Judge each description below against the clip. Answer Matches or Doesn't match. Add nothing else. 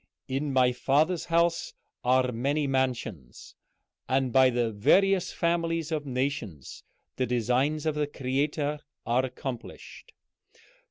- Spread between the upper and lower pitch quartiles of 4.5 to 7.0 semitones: Doesn't match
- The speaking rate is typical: Doesn't match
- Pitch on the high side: Doesn't match